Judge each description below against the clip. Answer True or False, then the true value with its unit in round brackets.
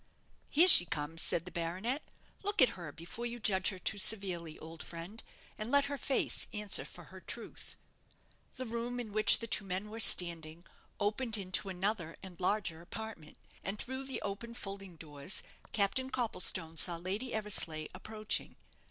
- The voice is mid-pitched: False (200 Hz)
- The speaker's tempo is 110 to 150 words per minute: False (165 wpm)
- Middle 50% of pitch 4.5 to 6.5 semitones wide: True (4.9 semitones)